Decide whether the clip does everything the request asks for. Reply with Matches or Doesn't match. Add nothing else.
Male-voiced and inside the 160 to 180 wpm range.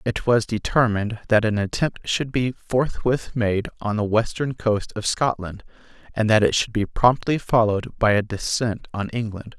Matches